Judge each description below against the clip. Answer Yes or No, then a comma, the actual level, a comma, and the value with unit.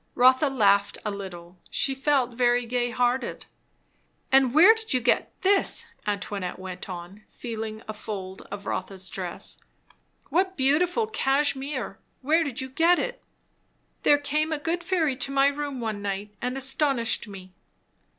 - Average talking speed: Yes, average, 150 wpm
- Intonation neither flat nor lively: No, wide, 6.1 semitones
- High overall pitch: Yes, very high, 255 Hz